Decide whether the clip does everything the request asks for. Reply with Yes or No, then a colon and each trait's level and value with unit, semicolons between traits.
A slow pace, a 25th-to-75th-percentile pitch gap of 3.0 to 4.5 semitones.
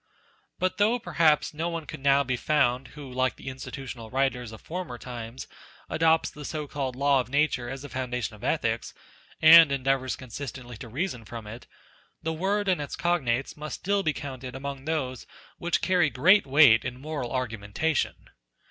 No: average, 175 wpm; average, 3.9 semitones